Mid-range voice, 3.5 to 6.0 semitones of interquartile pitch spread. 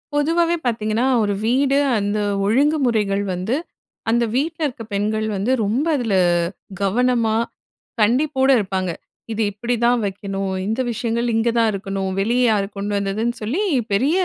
No: high, 225 Hz; average, 3.9 semitones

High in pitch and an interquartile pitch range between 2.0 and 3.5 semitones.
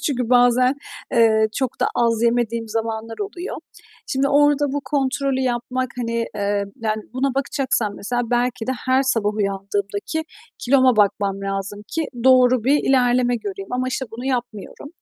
Yes: high, 245 Hz; average, 3.1 semitones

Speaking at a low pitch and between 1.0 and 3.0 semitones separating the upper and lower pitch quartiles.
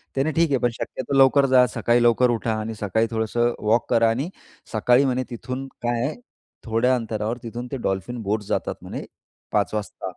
Yes: low, 120 Hz; narrow, 2.5 semitones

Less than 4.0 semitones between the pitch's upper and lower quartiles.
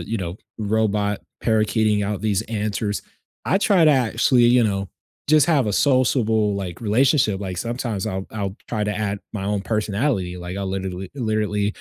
Yes: average, 2.9 semitones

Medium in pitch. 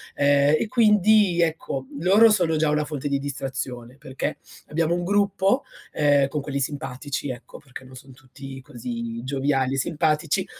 Yes: medium, 145 Hz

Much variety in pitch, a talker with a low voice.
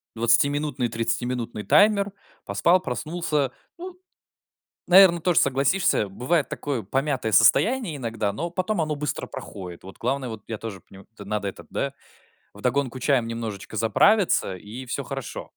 Yes: wide, 6.4 semitones; low, 130 Hz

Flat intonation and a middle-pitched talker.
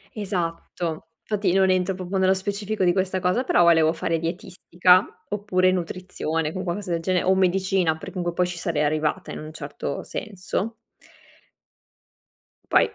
Yes: narrow, 2.3 semitones; medium, 180 Hz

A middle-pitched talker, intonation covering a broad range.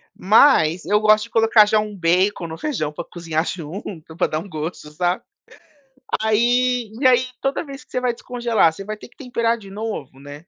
No: high, 210 Hz; wide, 5.9 semitones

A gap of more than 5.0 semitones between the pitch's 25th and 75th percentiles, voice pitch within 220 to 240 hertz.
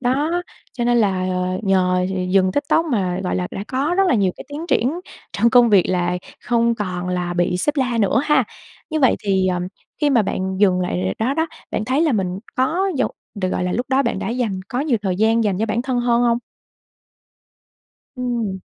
Yes: wide, 5.6 semitones; high, 225 Hz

